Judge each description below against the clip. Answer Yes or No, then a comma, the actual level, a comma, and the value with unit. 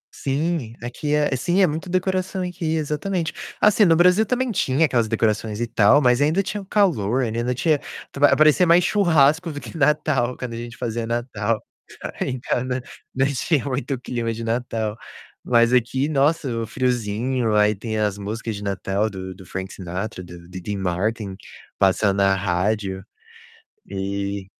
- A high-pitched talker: No, low, 120 Hz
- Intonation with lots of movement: Yes, wide, 6.4 semitones